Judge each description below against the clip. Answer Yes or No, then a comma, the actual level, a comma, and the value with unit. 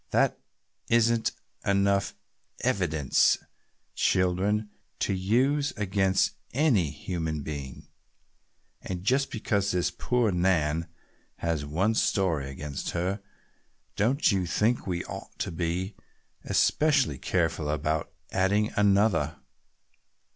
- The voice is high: No, very low, 95 Hz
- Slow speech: Yes, slow, 100 wpm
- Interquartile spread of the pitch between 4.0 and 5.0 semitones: Yes, average, 4.5 semitones